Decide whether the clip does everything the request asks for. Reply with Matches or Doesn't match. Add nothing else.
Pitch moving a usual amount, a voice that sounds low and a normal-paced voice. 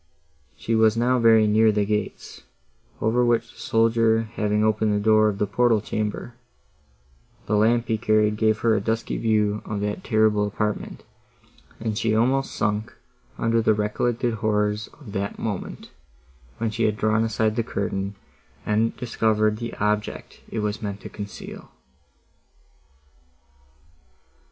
Doesn't match